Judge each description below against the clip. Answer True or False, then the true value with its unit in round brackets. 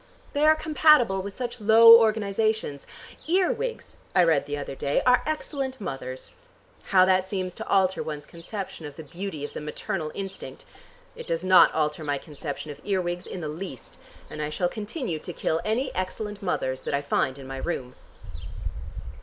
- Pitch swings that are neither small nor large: False (6.5 semitones)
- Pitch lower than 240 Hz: True (185 Hz)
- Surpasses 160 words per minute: True (175 wpm)